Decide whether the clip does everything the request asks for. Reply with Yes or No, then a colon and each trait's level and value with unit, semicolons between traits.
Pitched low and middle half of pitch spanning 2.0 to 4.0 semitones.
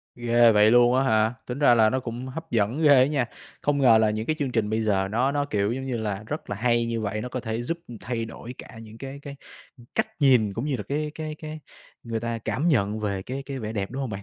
Yes: low, 120 Hz; average, 3.6 semitones